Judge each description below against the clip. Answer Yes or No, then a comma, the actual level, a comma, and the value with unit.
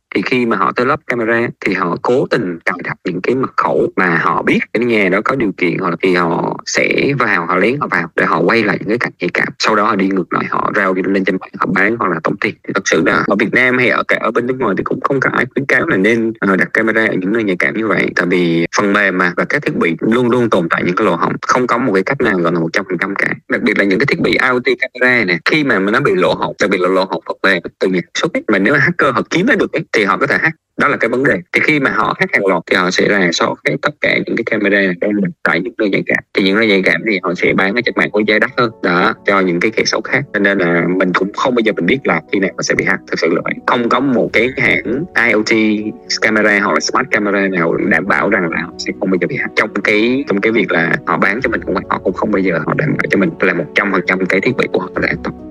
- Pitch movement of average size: Yes, average, 3.1 semitones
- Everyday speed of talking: No, fast, 320 wpm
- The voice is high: No, low, 100 Hz